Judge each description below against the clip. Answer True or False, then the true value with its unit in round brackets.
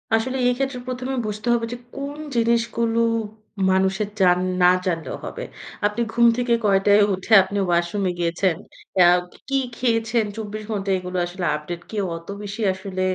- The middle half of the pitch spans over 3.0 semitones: True (4.0 semitones)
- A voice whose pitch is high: True (205 Hz)